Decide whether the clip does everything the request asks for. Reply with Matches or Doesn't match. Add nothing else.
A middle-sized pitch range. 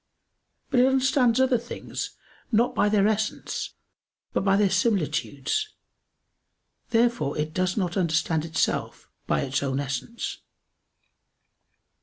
Doesn't match